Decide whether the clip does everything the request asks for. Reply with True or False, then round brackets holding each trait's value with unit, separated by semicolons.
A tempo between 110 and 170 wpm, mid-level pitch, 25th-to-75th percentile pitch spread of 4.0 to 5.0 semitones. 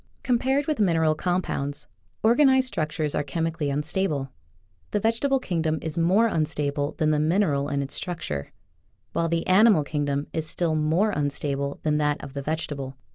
True (160 wpm; 155 Hz; 4.5 semitones)